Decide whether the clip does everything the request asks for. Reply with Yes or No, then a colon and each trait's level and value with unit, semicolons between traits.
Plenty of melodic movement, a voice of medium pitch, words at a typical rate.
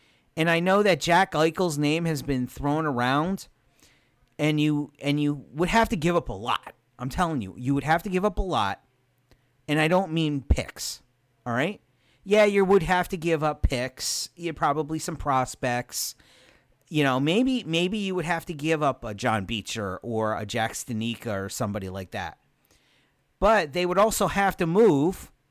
Yes: wide, 5.9 semitones; medium, 150 Hz; average, 190 wpm